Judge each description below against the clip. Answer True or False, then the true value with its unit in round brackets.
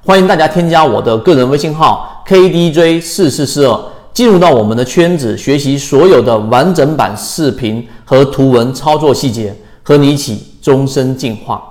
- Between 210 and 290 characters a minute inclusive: True (270 characters per minute)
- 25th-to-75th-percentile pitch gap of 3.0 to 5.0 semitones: False (5.5 semitones)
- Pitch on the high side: False (135 Hz)